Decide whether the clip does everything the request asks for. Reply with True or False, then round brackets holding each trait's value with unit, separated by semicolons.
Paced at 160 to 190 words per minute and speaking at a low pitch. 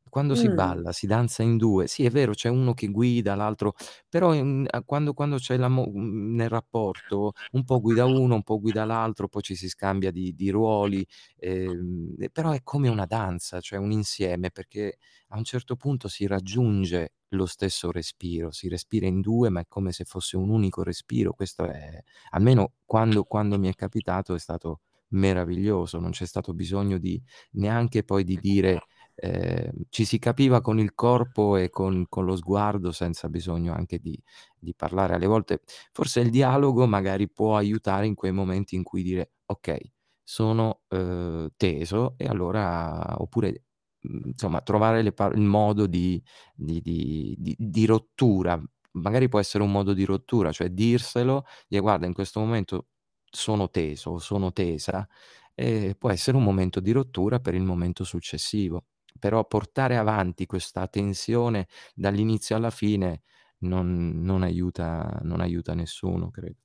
True (165 wpm; 100 Hz)